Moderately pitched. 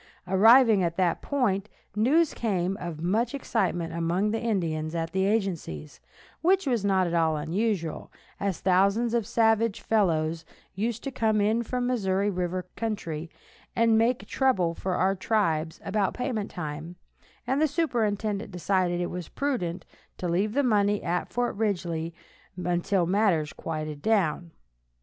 No: high, 195 Hz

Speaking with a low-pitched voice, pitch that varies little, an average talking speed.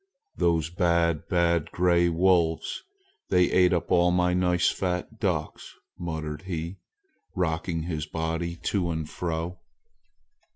No: very low, 85 Hz; narrow, 1.6 semitones; slow, 120 wpm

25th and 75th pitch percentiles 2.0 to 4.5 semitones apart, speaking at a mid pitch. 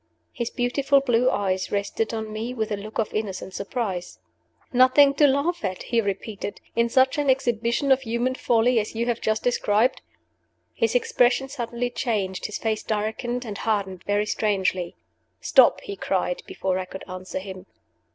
No: average, 3.8 semitones; high, 225 Hz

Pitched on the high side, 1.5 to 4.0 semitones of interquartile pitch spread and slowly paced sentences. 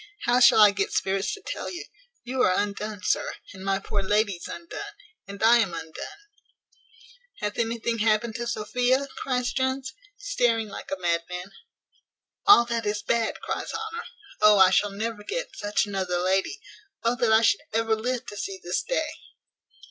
No: high, 220 Hz; average, 3.7 semitones; average, 170 wpm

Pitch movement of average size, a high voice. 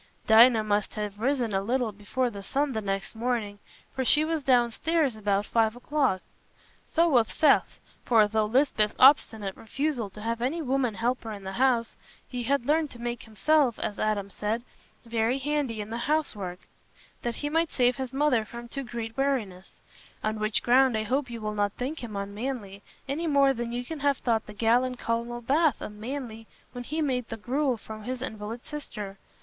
Yes: average, 3.9 semitones; high, 235 Hz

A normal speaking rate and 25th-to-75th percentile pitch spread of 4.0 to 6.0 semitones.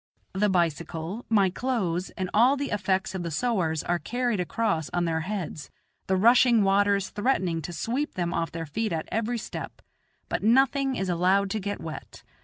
Yes: average, 180 wpm; average, 4.9 semitones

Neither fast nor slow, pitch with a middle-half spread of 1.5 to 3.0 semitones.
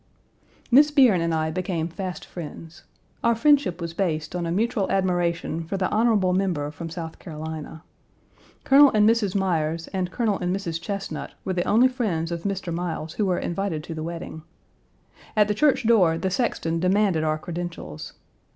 No: average, 170 wpm; average, 3.8 semitones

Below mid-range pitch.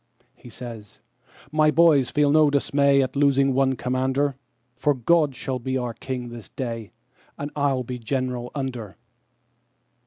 Yes: low, 130 Hz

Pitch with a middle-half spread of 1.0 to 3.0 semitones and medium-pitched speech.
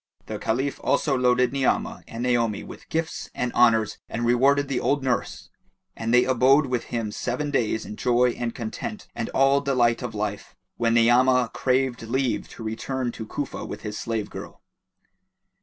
No: narrow, 2.6 semitones; low, 125 Hz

